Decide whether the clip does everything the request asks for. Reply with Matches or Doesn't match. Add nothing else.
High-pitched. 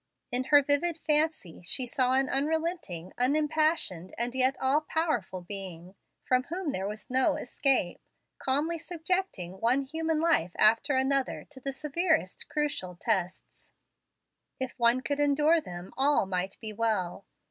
Matches